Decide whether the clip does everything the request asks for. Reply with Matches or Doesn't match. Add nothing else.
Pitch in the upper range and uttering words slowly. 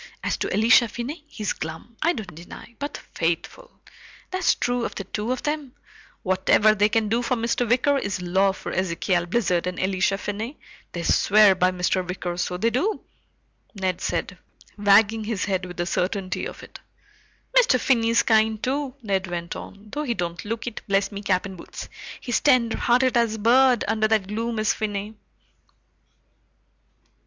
Doesn't match